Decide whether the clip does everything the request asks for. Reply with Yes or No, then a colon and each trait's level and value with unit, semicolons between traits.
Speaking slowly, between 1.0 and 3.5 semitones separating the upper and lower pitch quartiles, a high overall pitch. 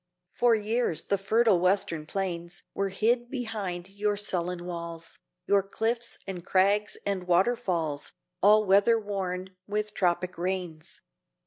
Yes: slow, 120 wpm; average, 3.0 semitones; high, 195 Hz